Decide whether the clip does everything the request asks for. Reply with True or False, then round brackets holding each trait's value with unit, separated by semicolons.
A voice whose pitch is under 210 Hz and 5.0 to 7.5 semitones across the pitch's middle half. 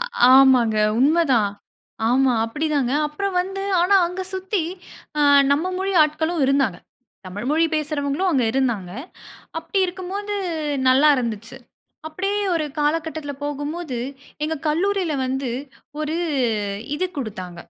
False (300 Hz; 5.3 semitones)